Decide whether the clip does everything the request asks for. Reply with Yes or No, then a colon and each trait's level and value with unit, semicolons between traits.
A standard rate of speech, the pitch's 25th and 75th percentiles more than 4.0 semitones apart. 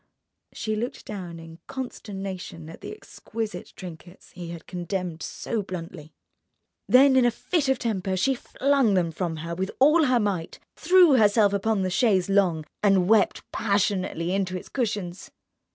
Yes: average, 160 wpm; average, 4.7 semitones